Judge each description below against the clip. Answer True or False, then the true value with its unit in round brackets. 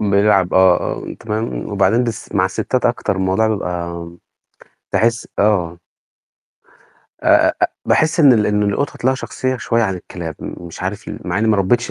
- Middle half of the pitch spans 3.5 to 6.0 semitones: True (3.8 semitones)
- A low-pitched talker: True (105 Hz)